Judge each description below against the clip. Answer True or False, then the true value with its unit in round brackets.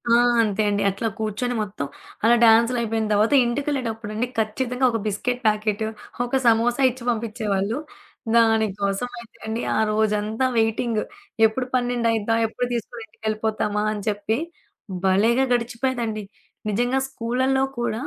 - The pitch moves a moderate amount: False (2.1 semitones)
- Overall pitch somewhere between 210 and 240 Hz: True (225 Hz)